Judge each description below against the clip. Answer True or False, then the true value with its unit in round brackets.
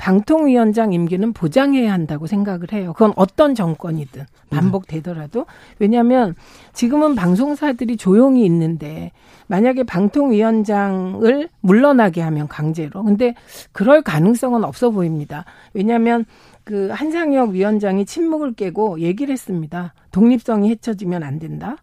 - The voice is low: False (205 Hz)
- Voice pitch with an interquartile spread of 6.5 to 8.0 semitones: False (5.6 semitones)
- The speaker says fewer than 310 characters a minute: False (325 characters per minute)